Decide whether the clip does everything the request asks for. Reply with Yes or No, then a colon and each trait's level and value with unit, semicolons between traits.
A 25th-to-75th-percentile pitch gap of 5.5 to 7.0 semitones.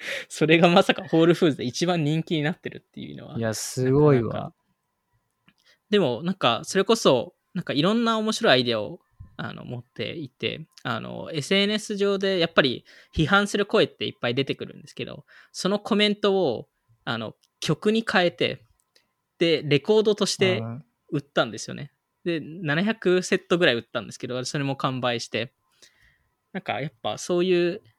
Yes: wide, 5.9 semitones